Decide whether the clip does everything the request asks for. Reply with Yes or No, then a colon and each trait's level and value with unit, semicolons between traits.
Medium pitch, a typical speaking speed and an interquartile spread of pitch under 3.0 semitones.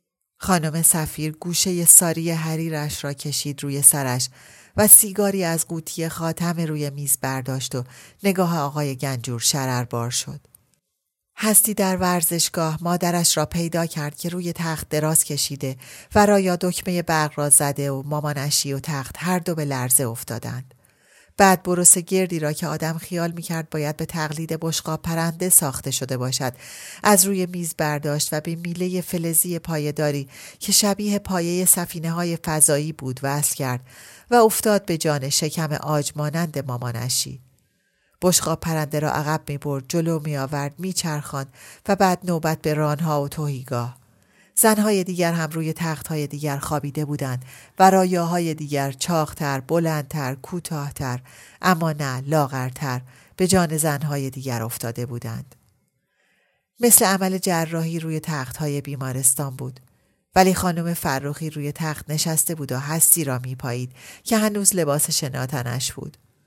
No: medium, 155 Hz; average, 140 wpm; average, 3.7 semitones